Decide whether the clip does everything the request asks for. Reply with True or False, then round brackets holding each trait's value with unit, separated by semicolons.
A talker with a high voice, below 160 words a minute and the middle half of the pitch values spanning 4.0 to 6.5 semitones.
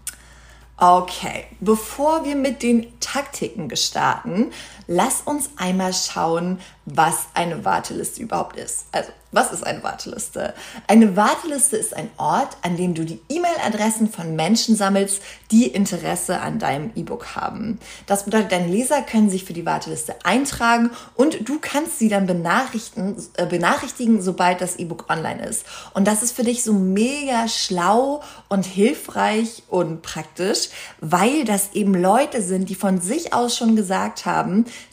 True (210 Hz; 150 wpm; 4.6 semitones)